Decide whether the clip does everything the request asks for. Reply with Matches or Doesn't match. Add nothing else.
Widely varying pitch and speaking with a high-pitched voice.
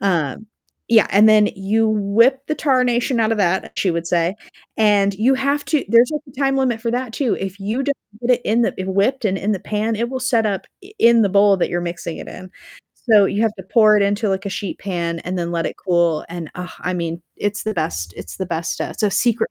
Doesn't match